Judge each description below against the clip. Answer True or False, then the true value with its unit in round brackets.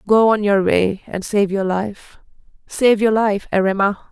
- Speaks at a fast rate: False (175 wpm)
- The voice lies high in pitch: True (205 Hz)